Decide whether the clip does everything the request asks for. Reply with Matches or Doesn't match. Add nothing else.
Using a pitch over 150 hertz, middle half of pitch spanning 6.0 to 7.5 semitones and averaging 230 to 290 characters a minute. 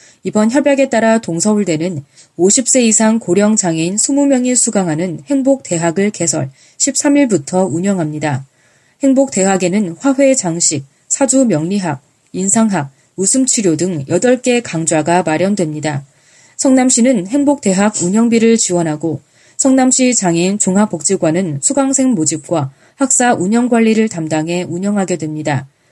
Matches